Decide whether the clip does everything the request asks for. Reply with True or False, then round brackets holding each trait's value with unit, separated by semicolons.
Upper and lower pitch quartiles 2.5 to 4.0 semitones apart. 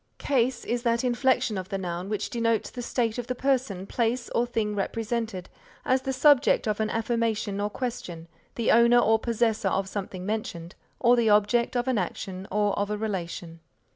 True (3.3 semitones)